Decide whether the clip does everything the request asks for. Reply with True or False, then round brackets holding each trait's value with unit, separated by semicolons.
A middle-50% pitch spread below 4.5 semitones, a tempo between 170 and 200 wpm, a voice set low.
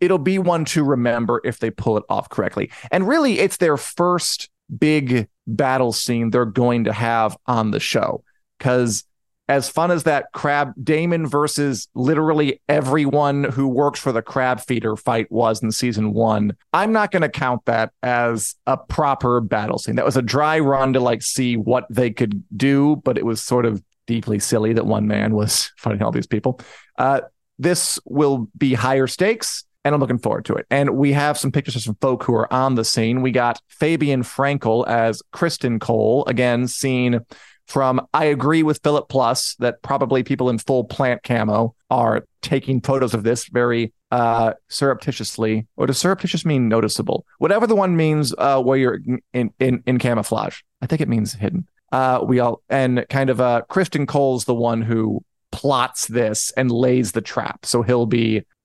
True (3.5 semitones; 185 wpm; 125 Hz)